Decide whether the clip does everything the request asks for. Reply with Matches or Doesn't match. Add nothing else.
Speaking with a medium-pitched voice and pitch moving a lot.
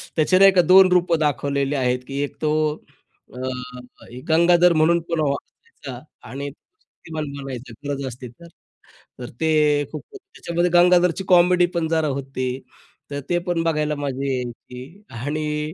Doesn't match